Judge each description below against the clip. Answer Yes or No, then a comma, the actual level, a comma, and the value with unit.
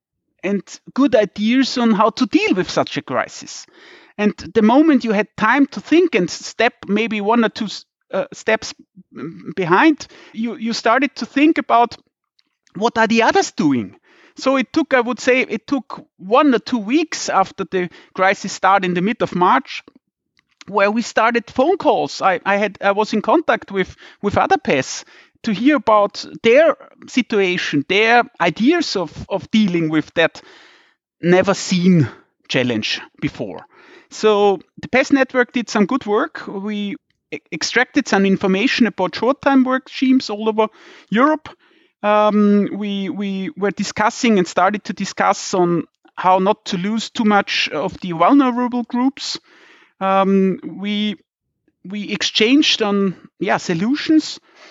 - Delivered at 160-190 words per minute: No, average, 150 wpm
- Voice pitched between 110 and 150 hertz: No, high, 220 Hz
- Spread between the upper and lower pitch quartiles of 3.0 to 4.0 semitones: No, average, 5.0 semitones